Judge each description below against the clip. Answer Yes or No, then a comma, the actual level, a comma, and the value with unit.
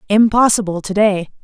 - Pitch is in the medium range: No, high, 205 Hz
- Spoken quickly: No, slow, 125 wpm